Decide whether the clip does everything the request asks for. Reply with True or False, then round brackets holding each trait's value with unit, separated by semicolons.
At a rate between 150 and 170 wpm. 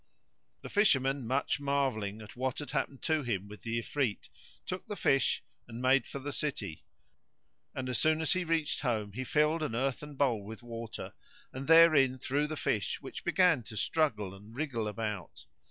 False (180 wpm)